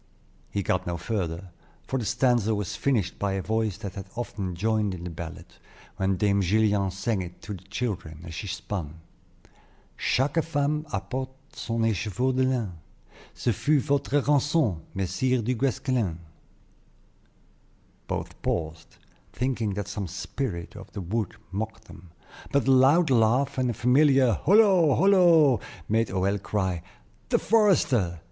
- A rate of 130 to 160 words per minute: Yes, average, 145 wpm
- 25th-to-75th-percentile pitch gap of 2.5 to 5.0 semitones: No, wide, 5.6 semitones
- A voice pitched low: Yes, low, 110 Hz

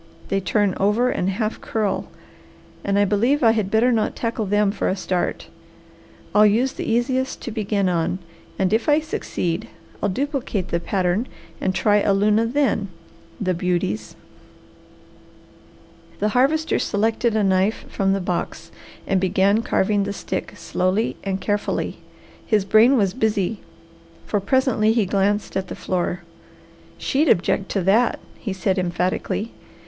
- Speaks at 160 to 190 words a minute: No, average, 150 wpm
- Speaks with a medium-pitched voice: No, high, 205 Hz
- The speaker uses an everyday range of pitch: Yes, average, 3.0 semitones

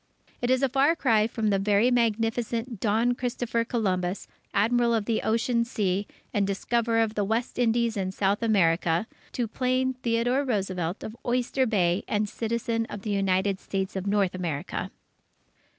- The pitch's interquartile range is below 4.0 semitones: Yes, average, 3.4 semitones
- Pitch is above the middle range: Yes, high, 225 Hz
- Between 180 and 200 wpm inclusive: No, average, 160 wpm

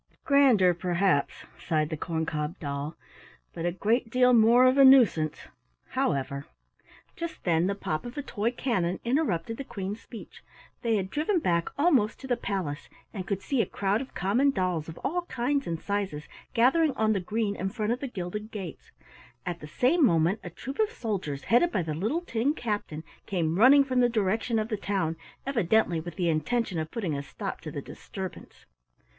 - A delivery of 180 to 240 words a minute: Yes, average, 190 wpm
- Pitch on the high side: Yes, high, 205 Hz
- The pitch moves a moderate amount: No, wide, 6.5 semitones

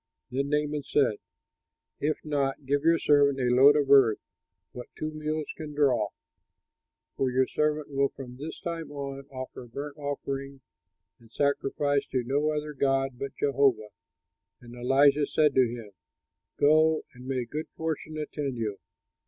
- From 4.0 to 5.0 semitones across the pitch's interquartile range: No, narrow, 2.4 semitones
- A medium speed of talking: Yes, average, 155 wpm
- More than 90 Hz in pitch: Yes, medium, 140 Hz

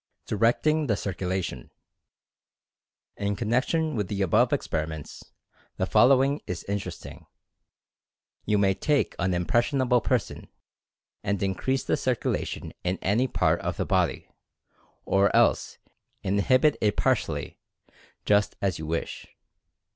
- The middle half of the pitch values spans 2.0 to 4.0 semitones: No, average, 5.2 semitones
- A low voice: Yes, low, 100 Hz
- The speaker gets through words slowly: Yes, slow, 120 wpm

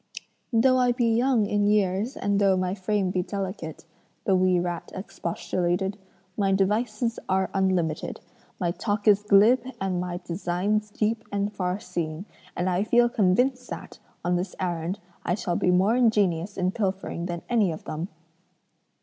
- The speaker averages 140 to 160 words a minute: Yes, average, 155 wpm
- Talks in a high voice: Yes, high, 195 Hz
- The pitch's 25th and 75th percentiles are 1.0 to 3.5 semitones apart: Yes, average, 2.8 semitones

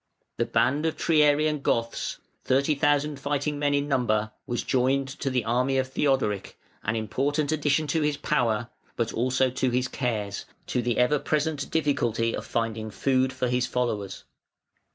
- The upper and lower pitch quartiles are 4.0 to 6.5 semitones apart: No, average, 3.5 semitones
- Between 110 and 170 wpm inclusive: Yes, average, 160 wpm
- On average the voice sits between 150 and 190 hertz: No, low, 130 Hz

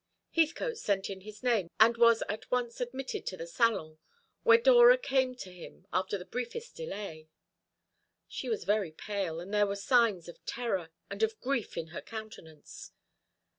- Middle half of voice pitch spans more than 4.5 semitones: Yes, average, 5.1 semitones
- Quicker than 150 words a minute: Yes, average, 170 wpm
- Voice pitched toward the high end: Yes, high, 215 Hz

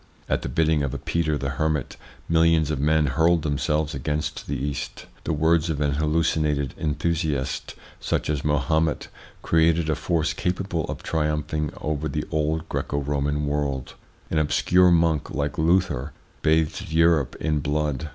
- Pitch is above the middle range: No, very low, 75 Hz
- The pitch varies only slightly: Yes, narrow, 1.8 semitones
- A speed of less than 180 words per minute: Yes, average, 155 wpm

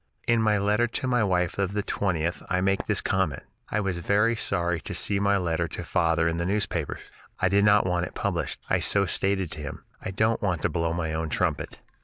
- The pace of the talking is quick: Yes, fast, 225 wpm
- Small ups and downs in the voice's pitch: No, average, 3.0 semitones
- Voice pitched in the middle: No, very low, 95 Hz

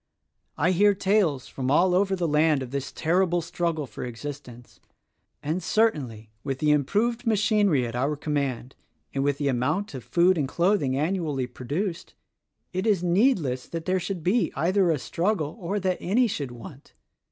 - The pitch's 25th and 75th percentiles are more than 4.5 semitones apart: Yes, wide, 5.5 semitones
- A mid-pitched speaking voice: Yes, medium, 165 Hz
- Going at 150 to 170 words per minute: Yes, average, 165 wpm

